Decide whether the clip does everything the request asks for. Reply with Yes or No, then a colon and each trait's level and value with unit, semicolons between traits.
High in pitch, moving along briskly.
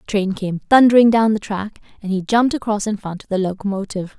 Yes: high, 205 Hz; fast, 230 wpm